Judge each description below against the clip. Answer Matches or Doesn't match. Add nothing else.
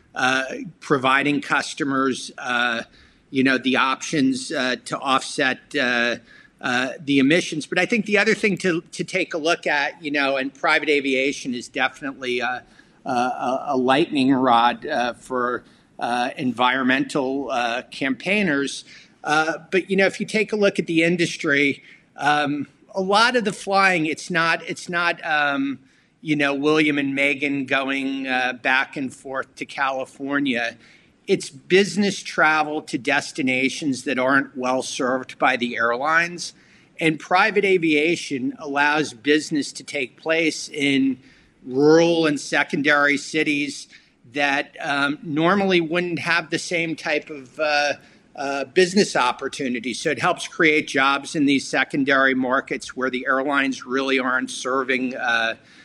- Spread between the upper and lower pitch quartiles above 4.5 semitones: Doesn't match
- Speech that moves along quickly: Doesn't match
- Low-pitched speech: Doesn't match